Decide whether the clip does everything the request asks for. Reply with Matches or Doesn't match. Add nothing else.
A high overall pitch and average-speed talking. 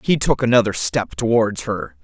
Doesn't match